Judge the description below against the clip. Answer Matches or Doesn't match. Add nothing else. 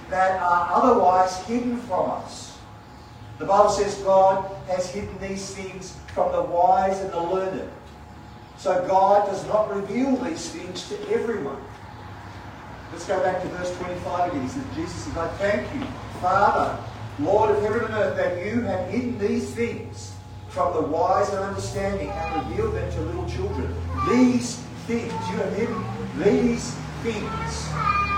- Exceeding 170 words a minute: Doesn't match